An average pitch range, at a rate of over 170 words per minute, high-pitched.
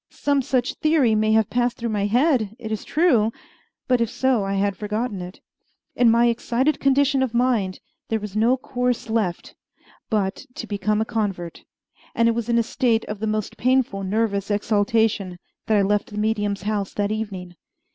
Yes: average, 3.0 semitones; average, 185 wpm; high, 220 Hz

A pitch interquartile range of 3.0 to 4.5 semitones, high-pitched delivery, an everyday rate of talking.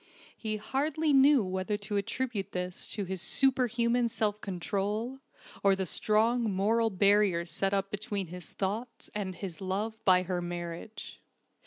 Yes: average, 3.4 semitones; high, 205 Hz; average, 145 wpm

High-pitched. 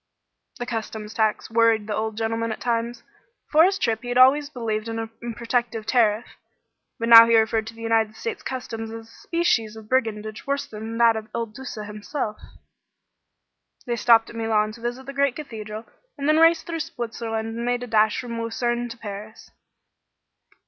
Yes: high, 230 Hz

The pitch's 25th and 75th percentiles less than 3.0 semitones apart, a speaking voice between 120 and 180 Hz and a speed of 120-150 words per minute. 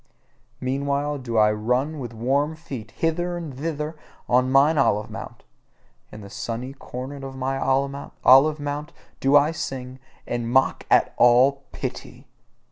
Yes: narrow, 2.6 semitones; low, 135 Hz; average, 140 wpm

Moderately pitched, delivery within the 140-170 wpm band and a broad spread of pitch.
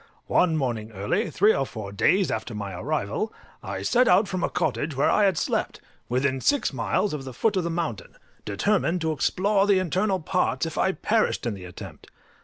No: medium, 160 Hz; average, 200 wpm; wide, 8.2 semitones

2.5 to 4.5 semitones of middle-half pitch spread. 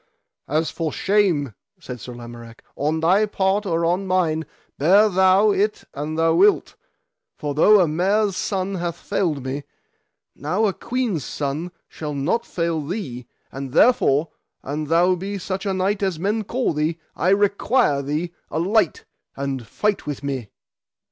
No: average, 5.1 semitones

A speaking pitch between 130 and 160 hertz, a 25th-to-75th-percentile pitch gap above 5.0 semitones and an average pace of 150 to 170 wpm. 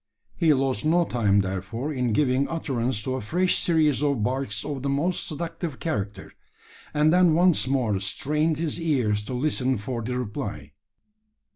Yes: low, 135 Hz; wide, 5.4 semitones; average, 160 wpm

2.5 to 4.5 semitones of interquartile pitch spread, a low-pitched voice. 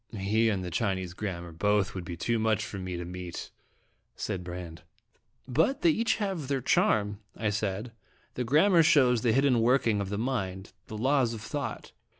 No: average, 5.1 semitones; low, 110 Hz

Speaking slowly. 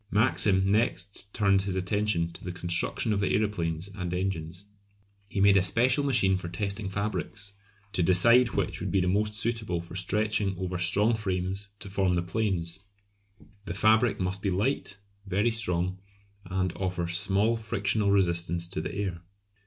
No: average, 160 wpm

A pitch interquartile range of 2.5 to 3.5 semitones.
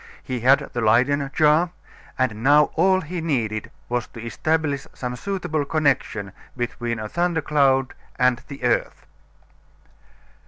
No: average, 4.3 semitones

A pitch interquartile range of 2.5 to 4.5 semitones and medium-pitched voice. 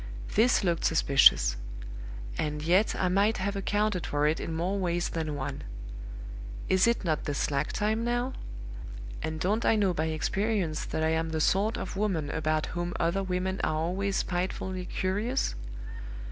Yes: average, 4.1 semitones; medium, 180 Hz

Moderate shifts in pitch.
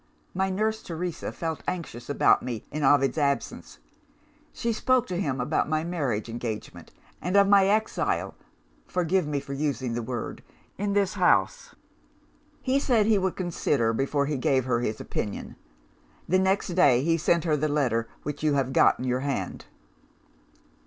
No: wide, 6.3 semitones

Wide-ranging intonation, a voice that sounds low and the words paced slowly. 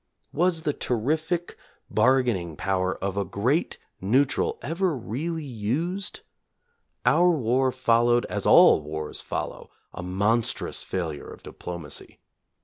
Yes: wide, 8.2 semitones; low, 120 Hz; slow, 120 wpm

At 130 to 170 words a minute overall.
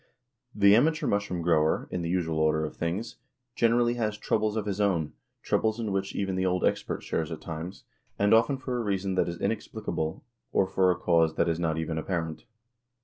No: average, 200 wpm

